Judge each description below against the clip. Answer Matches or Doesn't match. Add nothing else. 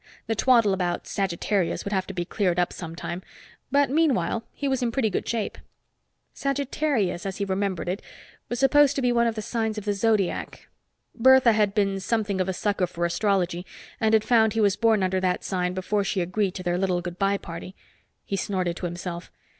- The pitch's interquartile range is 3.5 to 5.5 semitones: Matches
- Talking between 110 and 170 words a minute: Doesn't match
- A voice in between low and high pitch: Doesn't match